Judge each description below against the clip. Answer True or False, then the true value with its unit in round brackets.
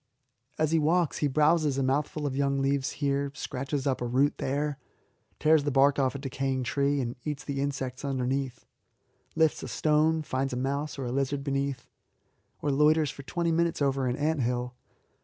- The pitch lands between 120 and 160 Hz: True (140 Hz)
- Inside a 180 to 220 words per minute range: True (190 wpm)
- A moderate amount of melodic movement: False (2.0 semitones)